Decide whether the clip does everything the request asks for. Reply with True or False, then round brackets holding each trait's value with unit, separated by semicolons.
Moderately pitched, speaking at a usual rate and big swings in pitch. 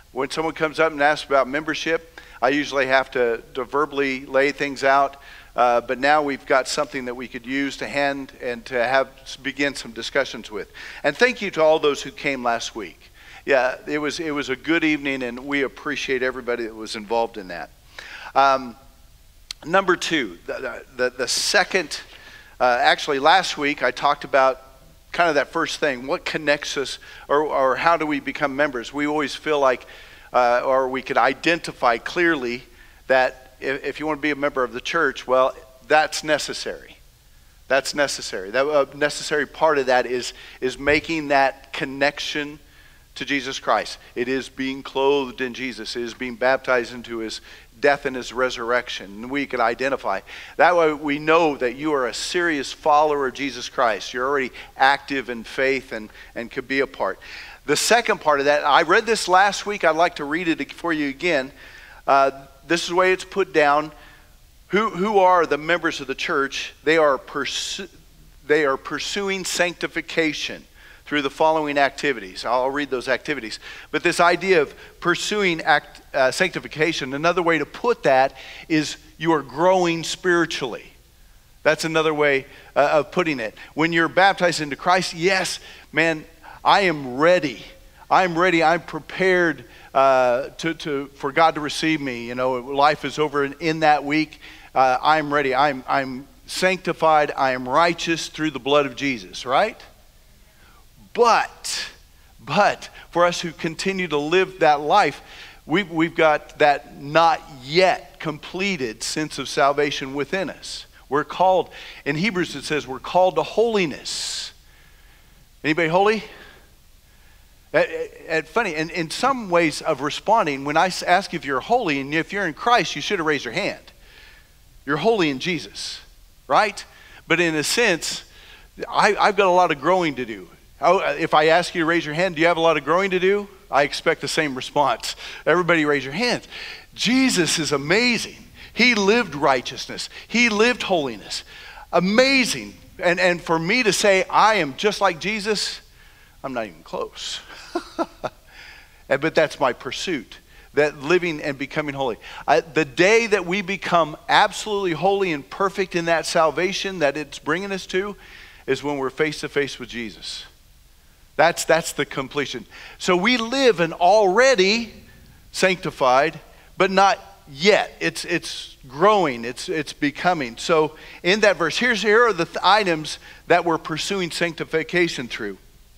False (155 Hz; 170 wpm; 4.6 semitones)